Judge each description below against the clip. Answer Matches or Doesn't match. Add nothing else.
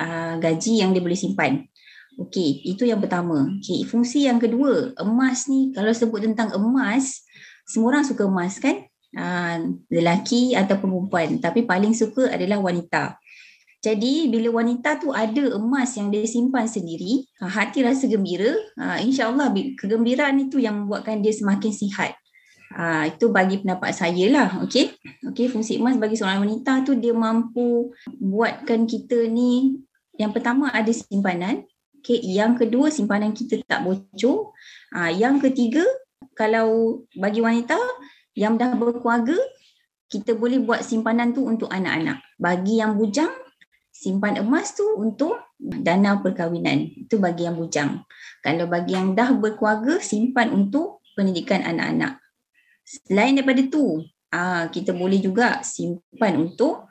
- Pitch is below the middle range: Doesn't match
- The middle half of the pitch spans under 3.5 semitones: Doesn't match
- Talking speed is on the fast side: Doesn't match